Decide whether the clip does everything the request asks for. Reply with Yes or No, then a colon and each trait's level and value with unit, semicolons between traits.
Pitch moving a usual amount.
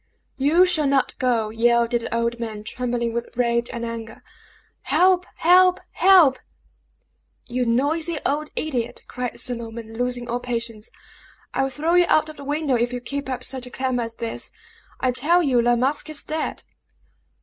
Yes: average, 4.1 semitones